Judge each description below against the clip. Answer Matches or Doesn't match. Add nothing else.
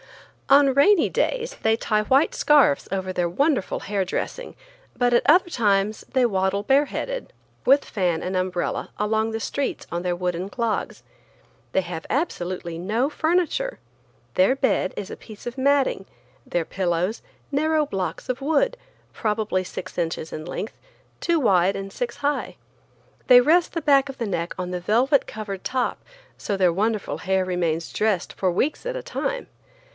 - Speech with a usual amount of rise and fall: Doesn't match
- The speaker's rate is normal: Matches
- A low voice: Doesn't match